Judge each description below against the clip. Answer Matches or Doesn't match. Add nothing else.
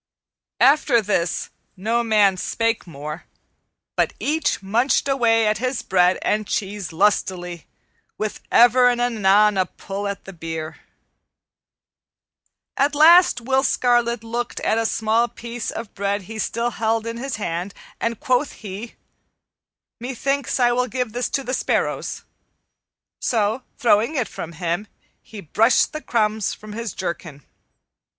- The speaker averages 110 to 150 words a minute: Matches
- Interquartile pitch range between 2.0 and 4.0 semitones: Matches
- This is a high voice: Matches